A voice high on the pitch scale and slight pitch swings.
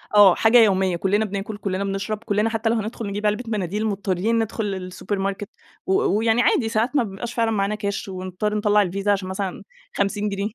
Yes: high, 205 Hz; narrow, 2.2 semitones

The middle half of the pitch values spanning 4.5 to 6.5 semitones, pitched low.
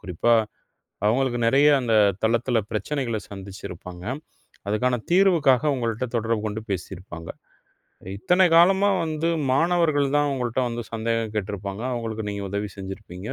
Yes: average, 4.9 semitones; low, 115 Hz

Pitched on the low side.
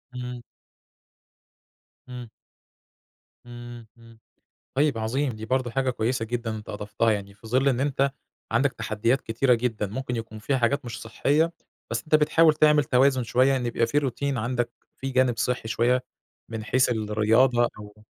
Yes: low, 120 Hz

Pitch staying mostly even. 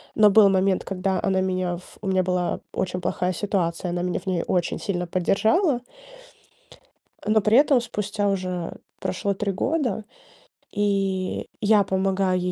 Yes: narrow, 2.2 semitones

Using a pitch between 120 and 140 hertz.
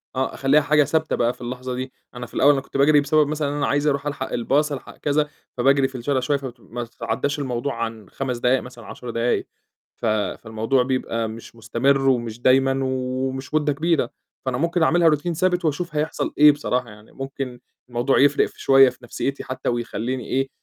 Yes: low, 135 Hz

